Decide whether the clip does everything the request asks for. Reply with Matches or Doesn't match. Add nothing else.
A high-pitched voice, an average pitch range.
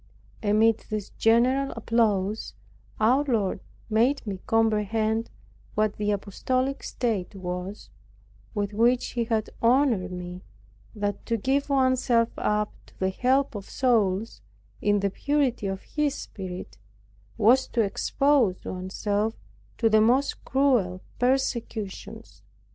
Matches